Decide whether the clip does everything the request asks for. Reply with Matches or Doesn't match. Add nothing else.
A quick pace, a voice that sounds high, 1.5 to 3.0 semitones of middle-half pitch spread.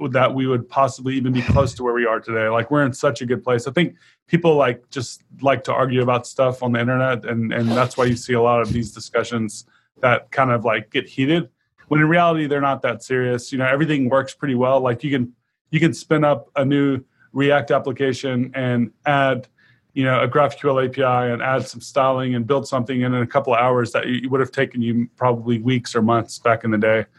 Doesn't match